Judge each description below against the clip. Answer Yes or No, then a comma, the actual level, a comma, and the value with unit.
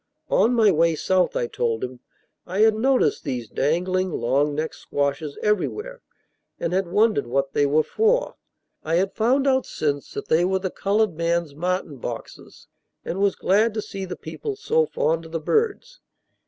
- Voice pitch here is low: No, medium, 180 Hz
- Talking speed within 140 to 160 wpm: No, average, 175 wpm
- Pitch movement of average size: No, wide, 6.4 semitones